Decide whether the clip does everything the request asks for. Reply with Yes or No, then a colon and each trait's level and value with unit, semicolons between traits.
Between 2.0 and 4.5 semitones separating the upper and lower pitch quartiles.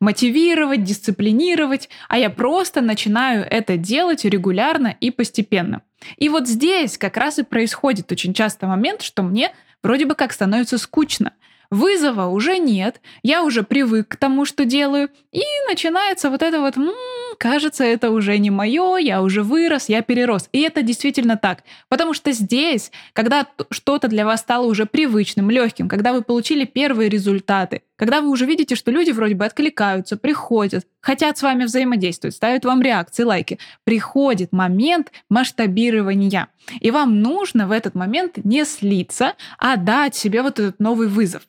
No: average, 5.2 semitones